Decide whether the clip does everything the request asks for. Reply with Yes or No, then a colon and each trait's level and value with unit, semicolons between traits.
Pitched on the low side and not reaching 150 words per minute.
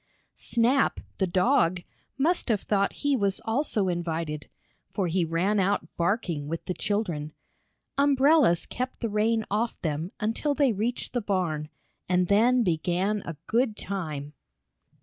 No: high, 200 Hz; average, 140 wpm